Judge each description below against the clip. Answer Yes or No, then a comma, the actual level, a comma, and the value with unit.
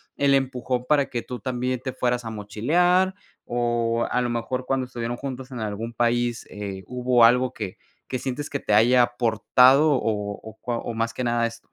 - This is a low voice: Yes, low, 120 Hz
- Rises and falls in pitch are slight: Yes, narrow, 1.8 semitones